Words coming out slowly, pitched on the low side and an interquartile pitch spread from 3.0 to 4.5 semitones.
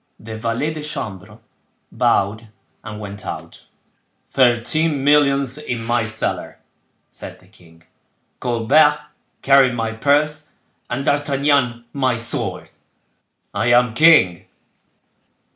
Yes: slow, 100 wpm; low, 120 Hz; average, 4.2 semitones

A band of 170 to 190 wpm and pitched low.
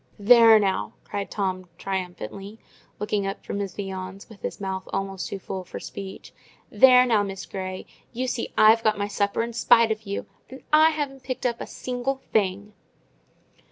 No: average, 175 wpm; high, 205 Hz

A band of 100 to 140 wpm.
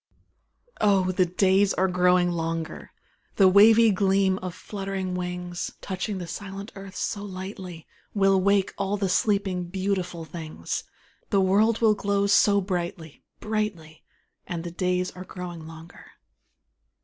Yes: slow, 135 wpm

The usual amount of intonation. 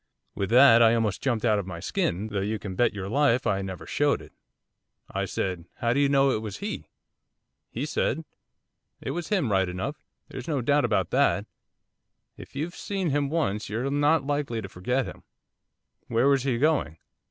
No: wide, 6.0 semitones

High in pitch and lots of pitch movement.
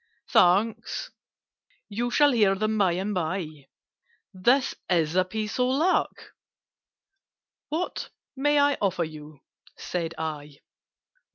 Yes: high, 195 Hz; wide, 7.1 semitones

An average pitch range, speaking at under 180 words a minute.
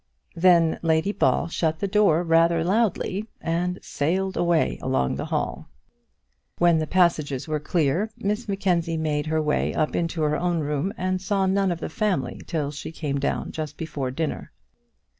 Yes: average, 3.2 semitones; average, 165 wpm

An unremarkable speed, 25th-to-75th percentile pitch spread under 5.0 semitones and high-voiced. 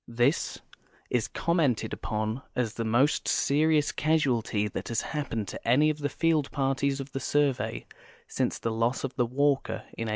No: average, 170 wpm; average, 4.1 semitones; low, 135 Hz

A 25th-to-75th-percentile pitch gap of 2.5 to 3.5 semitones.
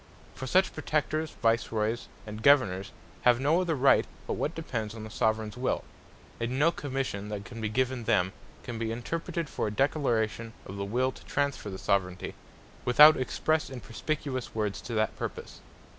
No: average, 4.7 semitones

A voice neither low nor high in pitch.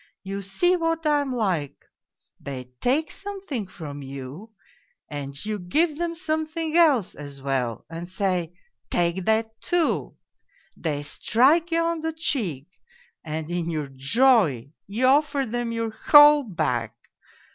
No: high, 215 Hz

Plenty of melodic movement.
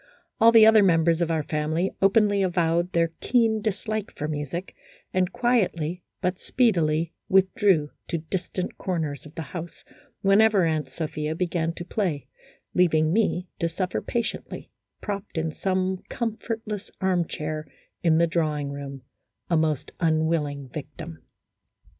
No: average, 3.8 semitones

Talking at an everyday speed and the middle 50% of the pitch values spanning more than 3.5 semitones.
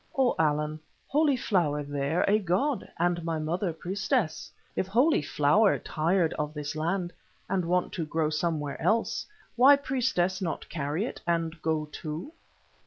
Yes: average, 150 wpm; average, 4.5 semitones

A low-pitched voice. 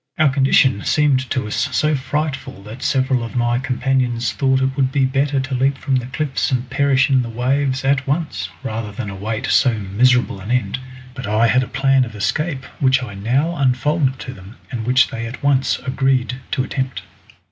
Yes: low, 130 Hz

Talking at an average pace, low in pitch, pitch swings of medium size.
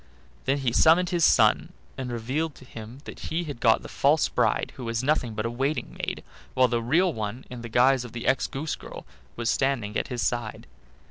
No: fast, 215 wpm; low, 125 Hz; average, 3.2 semitones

